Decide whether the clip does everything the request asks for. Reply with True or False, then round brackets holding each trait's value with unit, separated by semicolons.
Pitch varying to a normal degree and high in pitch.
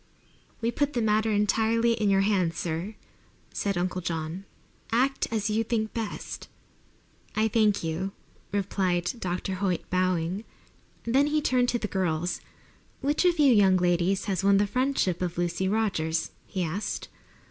True (3.9 semitones; 200 Hz)